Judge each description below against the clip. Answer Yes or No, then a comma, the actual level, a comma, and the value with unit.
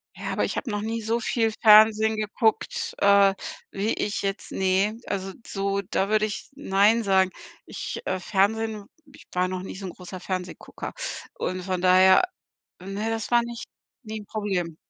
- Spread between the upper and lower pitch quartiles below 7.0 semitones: Yes, narrow, 2.5 semitones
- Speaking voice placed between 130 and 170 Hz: No, high, 200 Hz